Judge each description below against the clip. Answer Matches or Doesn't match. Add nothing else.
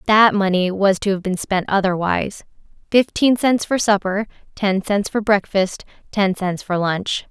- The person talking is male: Doesn't match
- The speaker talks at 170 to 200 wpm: Doesn't match